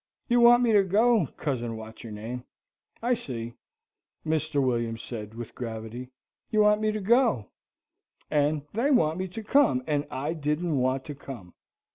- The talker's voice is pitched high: No, medium, 145 Hz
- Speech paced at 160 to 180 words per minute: Yes, average, 165 wpm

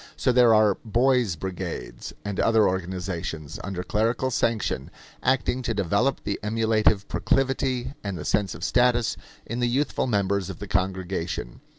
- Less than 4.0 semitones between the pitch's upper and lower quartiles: No, average, 4.5 semitones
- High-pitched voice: No, low, 105 Hz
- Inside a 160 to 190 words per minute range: No, average, 150 wpm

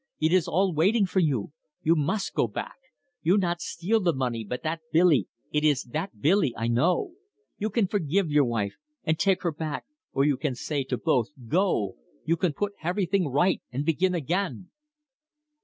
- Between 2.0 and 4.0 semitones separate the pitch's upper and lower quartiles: No, average, 4.8 semitones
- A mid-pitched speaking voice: Yes, medium, 165 Hz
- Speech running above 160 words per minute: Yes, average, 185 wpm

